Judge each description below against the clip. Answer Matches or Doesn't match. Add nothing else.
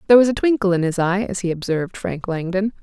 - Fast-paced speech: Matches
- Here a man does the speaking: Doesn't match